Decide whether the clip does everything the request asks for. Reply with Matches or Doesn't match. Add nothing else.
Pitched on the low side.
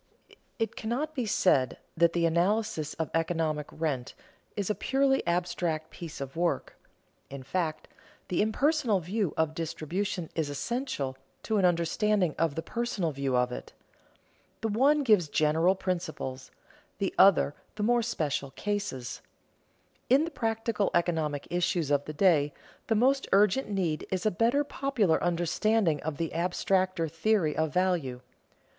Doesn't match